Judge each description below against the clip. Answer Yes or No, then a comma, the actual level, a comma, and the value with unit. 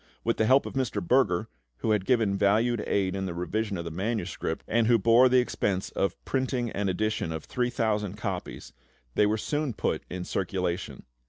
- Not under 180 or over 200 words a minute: Yes, average, 185 wpm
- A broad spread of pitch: No, average, 4.0 semitones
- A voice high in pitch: No, low, 105 Hz